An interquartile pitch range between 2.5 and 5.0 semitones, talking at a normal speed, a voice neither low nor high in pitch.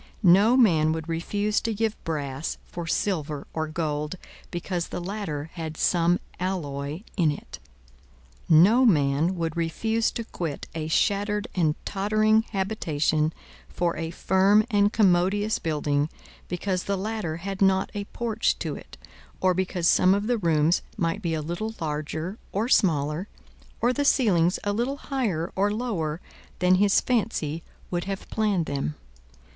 Yes: average, 4.5 semitones; average, 150 wpm; medium, 180 Hz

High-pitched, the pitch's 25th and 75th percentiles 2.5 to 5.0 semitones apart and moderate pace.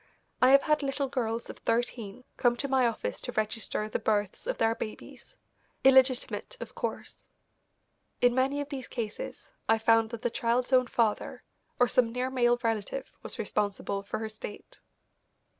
Yes: high, 240 Hz; average, 2.8 semitones; average, 165 wpm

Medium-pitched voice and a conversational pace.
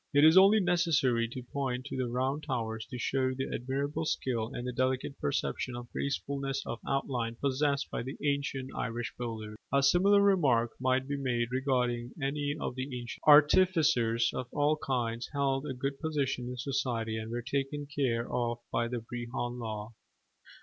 No: low, 130 Hz; average, 175 wpm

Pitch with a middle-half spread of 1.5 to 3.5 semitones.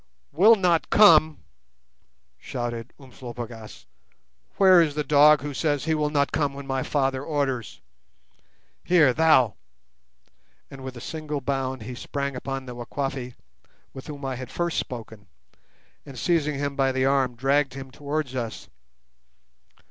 Yes: average, 2.8 semitones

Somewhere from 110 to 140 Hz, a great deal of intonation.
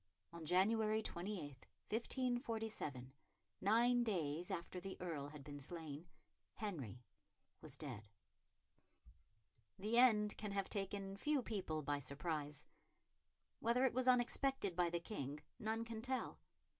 No: high, 195 Hz; wide, 6.9 semitones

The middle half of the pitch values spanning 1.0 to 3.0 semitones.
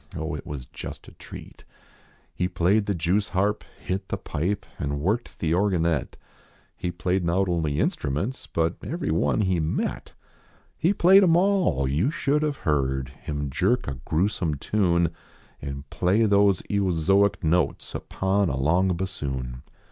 No: average, 5.1 semitones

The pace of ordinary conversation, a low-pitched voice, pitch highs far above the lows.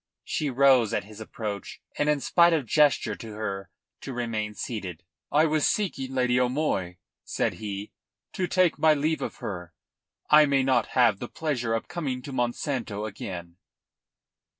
Yes: average, 160 wpm; low, 125 Hz; wide, 5.7 semitones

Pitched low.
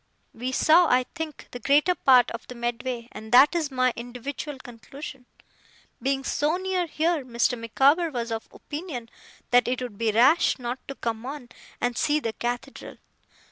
No: very high, 255 Hz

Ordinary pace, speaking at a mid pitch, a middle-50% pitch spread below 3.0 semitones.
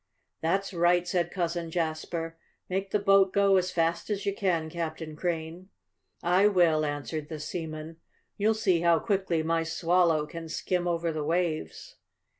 Yes: average, 155 wpm; medium, 170 Hz; narrow, 2.4 semitones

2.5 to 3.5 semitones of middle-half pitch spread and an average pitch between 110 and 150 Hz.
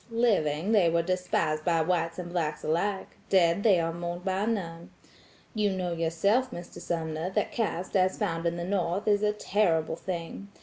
No: average, 3.2 semitones; medium, 175 Hz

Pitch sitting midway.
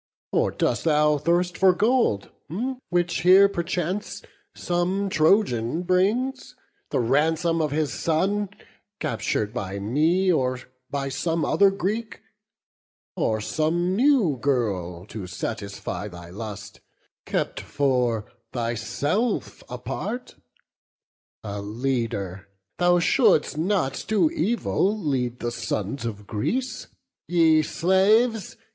Yes: medium, 155 Hz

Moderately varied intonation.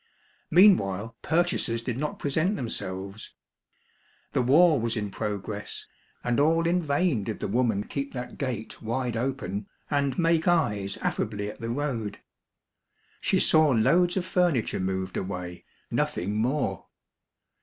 No: wide, 6.7 semitones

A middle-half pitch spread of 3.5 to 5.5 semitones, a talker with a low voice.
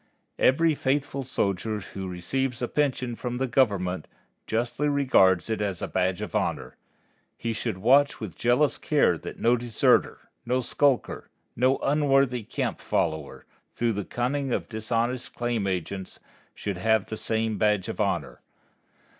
Yes: average, 4.6 semitones; low, 120 Hz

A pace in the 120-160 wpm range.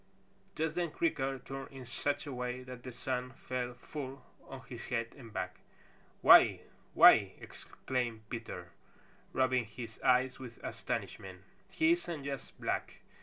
Yes: average, 145 wpm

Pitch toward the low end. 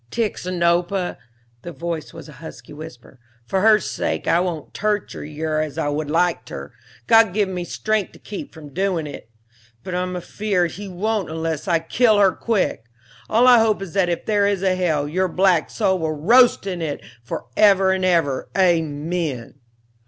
No: medium, 180 Hz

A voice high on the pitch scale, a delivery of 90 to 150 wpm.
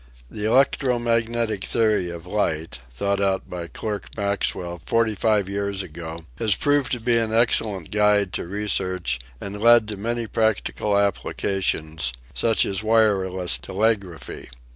No: low, 100 Hz; average, 140 wpm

